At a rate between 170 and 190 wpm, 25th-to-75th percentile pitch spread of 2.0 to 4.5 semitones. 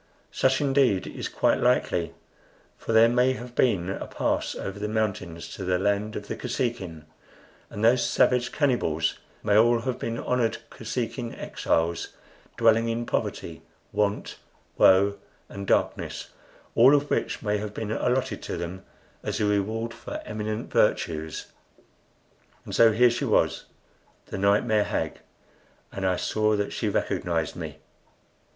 No: average, 145 wpm; average, 3.3 semitones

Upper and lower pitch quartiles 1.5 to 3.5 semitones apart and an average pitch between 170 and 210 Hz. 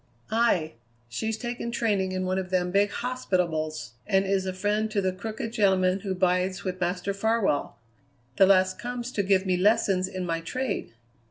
Yes: average, 2.9 semitones; high, 190 Hz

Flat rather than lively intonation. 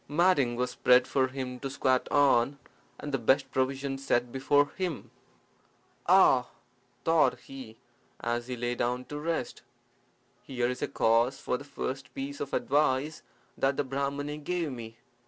Yes: narrow, 2.3 semitones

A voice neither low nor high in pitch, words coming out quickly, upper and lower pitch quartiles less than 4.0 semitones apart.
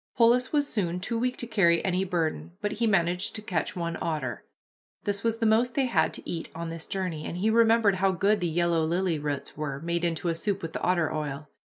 No: medium, 180 Hz; fast, 235 wpm; average, 4.6 semitones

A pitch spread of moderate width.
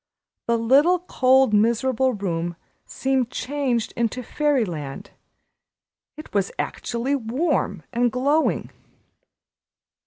Yes: average, 3.7 semitones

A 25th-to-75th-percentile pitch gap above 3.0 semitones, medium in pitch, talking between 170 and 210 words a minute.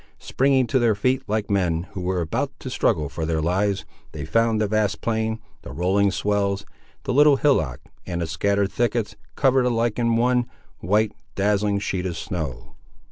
No: average, 4.4 semitones; low, 100 Hz; average, 175 wpm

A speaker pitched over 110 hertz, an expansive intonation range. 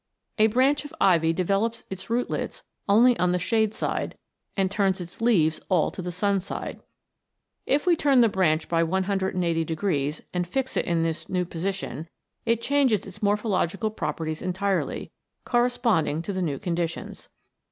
No: high, 190 Hz; average, 4.8 semitones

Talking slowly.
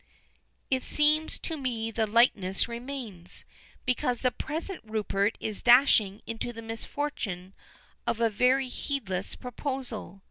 Yes: slow, 120 wpm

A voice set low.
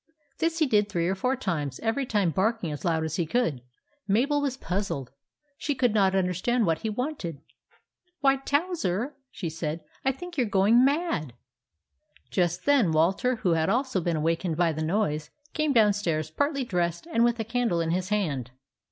No: high, 200 Hz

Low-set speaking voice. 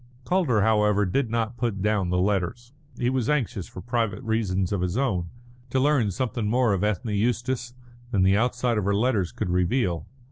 Yes: low, 110 Hz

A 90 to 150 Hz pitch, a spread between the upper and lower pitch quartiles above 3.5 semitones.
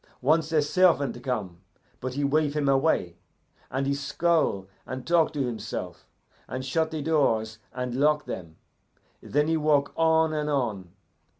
Yes: medium, 140 Hz; average, 3.9 semitones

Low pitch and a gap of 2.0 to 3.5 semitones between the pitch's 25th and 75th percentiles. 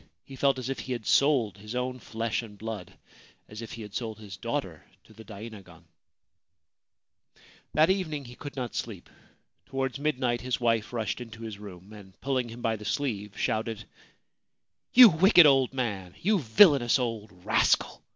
No: low, 115 Hz; average, 3.9 semitones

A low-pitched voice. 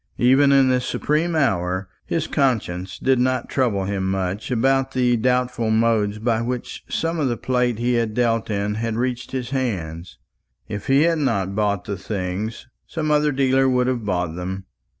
Yes: low, 120 Hz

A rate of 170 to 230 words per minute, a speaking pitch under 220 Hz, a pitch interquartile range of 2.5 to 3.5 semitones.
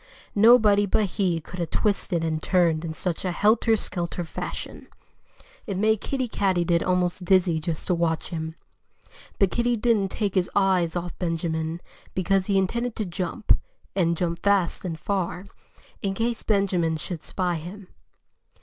No: average, 155 wpm; medium, 185 Hz; average, 3.0 semitones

